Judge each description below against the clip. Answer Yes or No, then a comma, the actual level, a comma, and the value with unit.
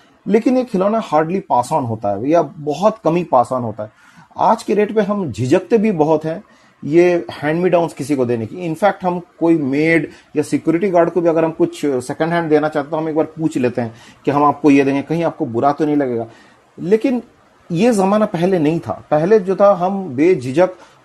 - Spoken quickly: Yes, fast, 215 wpm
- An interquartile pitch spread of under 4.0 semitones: No, average, 4.5 semitones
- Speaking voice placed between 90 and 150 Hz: No, medium, 160 Hz